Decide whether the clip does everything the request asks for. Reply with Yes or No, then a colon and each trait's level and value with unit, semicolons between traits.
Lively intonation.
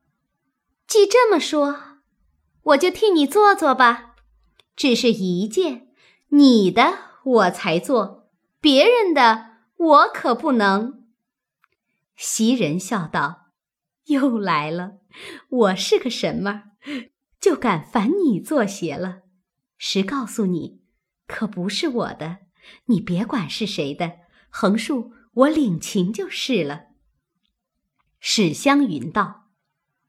Yes: wide, 6.7 semitones